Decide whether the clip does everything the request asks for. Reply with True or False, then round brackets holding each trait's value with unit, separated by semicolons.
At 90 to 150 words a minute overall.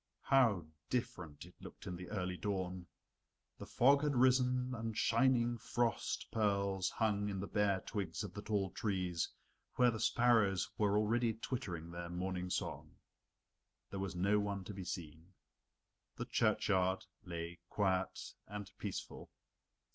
True (140 wpm)